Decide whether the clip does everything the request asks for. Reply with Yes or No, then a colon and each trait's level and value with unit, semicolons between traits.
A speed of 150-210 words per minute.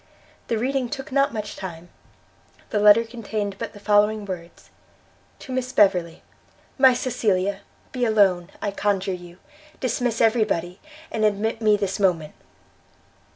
No: average, 140 wpm